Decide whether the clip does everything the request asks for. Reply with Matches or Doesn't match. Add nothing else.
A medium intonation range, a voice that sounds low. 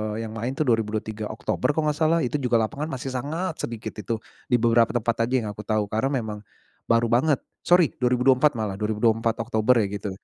Matches